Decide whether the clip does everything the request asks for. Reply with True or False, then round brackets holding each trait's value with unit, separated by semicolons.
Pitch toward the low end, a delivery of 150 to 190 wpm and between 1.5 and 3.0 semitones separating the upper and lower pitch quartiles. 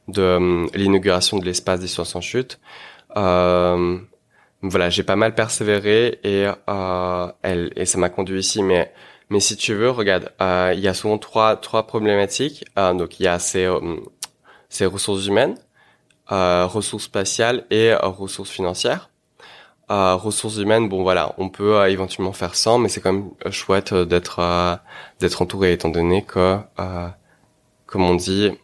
True (95 Hz; 170 wpm; 2.4 semitones)